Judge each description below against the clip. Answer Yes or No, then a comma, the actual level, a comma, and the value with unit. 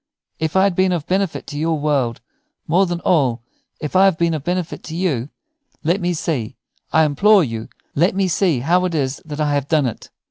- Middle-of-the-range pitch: Yes, medium, 160 Hz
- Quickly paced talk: Yes, fast, 215 wpm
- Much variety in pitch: No, average, 4.0 semitones